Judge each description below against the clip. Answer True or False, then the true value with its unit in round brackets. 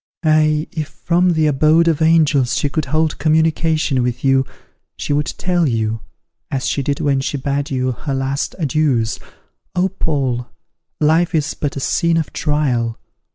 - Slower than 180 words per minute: True (160 wpm)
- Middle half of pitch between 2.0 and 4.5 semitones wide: True (3.1 semitones)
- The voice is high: False (145 Hz)